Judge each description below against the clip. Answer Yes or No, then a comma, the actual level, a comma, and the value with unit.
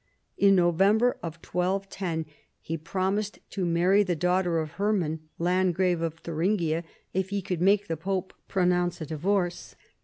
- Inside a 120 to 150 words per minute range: Yes, average, 140 wpm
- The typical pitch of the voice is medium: Yes, medium, 180 Hz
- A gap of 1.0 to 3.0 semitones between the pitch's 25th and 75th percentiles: Yes, narrow, 2.6 semitones